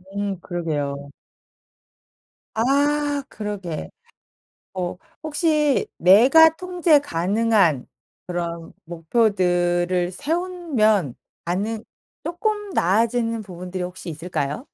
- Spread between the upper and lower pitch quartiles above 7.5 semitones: Yes, wide, 8.4 semitones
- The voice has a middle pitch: No, high, 205 Hz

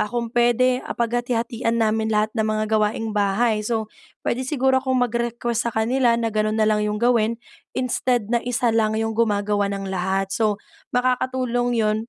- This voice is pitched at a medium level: No, high, 225 Hz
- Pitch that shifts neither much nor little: No, narrow, 2.2 semitones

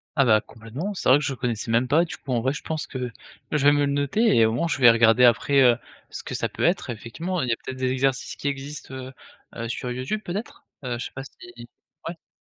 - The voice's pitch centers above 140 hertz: No, low, 130 Hz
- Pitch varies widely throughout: No, average, 3.3 semitones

